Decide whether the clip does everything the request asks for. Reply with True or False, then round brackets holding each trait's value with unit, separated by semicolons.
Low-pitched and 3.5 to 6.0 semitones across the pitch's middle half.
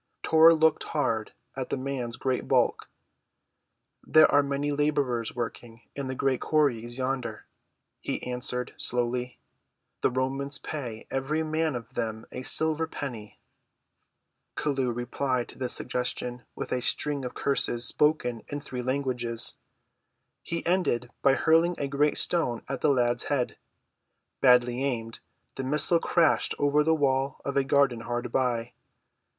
False (130 Hz; 3.0 semitones)